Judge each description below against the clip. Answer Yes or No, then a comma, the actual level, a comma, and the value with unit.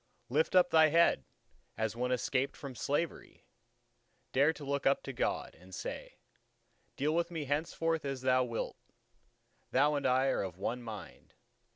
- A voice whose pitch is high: No, low, 135 Hz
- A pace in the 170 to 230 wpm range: No, average, 155 wpm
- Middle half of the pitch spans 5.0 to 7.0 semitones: No, average, 3.7 semitones